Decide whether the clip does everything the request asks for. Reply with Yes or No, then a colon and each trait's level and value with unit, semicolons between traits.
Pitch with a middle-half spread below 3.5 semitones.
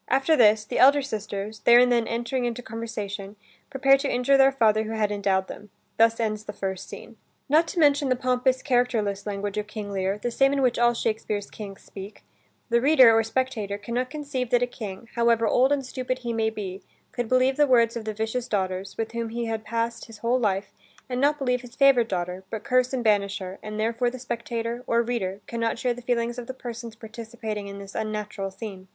Yes: average, 3.0 semitones